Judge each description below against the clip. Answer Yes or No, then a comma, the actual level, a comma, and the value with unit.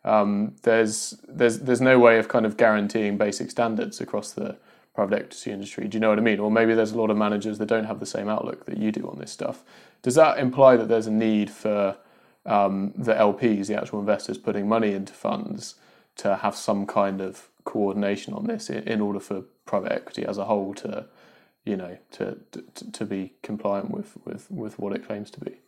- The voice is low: Yes, low, 105 Hz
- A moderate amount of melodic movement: No, narrow, 2.0 semitones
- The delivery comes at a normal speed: No, fast, 220 wpm